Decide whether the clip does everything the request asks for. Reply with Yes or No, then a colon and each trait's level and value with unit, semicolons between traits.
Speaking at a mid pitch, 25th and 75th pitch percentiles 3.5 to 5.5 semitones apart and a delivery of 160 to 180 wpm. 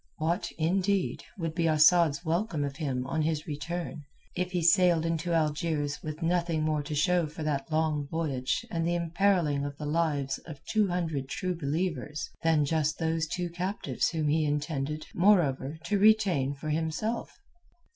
No: medium, 160 Hz; average, 2.7 semitones; average, 165 wpm